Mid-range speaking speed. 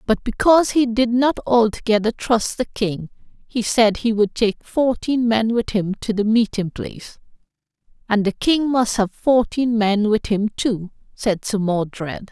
Yes: average, 170 wpm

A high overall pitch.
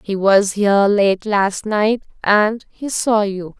Yes: high, 205 Hz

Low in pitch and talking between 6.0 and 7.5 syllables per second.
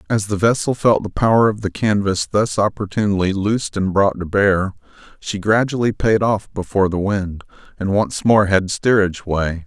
No: low, 100 Hz; 5.0 syllables/s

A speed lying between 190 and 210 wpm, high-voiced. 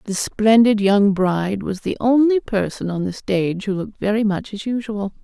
Yes: average, 195 wpm; high, 210 Hz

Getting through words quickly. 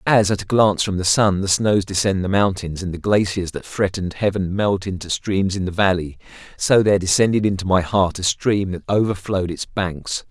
Yes: fast, 210 wpm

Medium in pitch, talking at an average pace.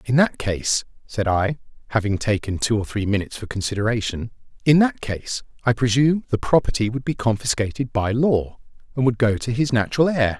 No: low, 115 Hz; average, 180 wpm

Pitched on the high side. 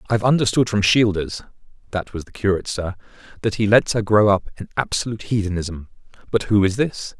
No: low, 105 Hz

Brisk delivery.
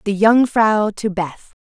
No: average, 145 wpm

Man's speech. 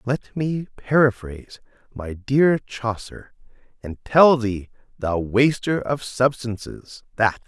Yes: male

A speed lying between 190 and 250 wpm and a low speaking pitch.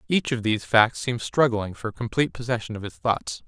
Yes: fast, 205 wpm; low, 115 Hz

